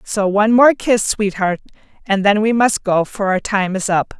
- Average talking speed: No, fast, 215 wpm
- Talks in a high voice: Yes, high, 205 Hz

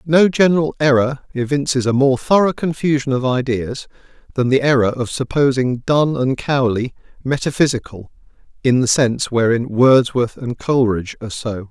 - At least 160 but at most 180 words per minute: No, average, 145 wpm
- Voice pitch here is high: No, low, 130 Hz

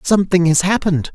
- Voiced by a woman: No, male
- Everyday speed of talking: Yes, average, 155 wpm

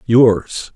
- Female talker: No, male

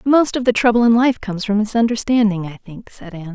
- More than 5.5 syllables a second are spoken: Yes, 6.2 syllables/s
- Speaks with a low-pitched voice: No, high, 220 Hz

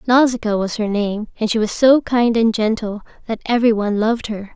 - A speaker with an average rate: No, fast, 210 wpm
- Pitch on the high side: Yes, high, 220 Hz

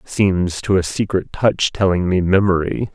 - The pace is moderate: Yes, average, 165 wpm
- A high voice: No, very low, 95 Hz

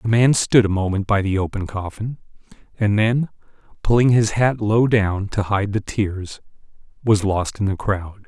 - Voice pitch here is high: No, low, 105 Hz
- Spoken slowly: No, average, 180 wpm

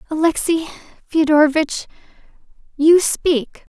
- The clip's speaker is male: No, female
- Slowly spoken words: Yes, slow, 65 wpm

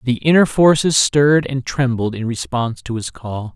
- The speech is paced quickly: No, average, 185 wpm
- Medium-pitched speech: No, low, 130 Hz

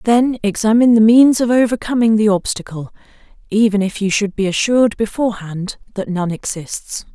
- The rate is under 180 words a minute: Yes, average, 150 wpm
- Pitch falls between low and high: No, high, 215 Hz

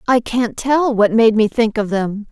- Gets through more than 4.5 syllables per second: No, 4.2 syllables/s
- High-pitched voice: Yes, high, 225 Hz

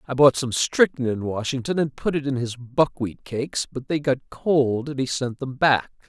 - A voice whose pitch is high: No, low, 135 Hz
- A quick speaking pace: Yes, fast, 215 wpm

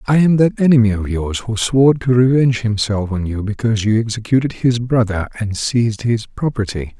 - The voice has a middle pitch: No, low, 115 Hz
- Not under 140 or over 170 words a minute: No, average, 190 wpm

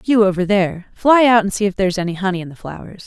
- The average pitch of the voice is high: Yes, high, 195 Hz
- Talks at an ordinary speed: No, fast, 295 wpm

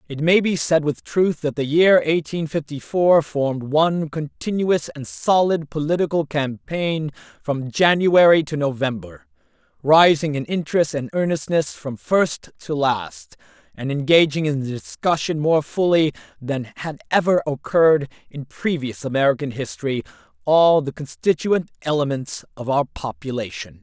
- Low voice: No, medium, 150 Hz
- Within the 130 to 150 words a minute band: Yes, slow, 135 wpm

